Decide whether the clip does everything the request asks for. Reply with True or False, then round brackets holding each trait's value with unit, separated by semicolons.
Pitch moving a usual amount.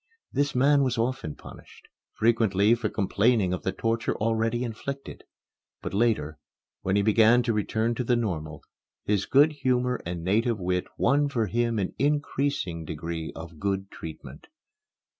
True (4.8 semitones)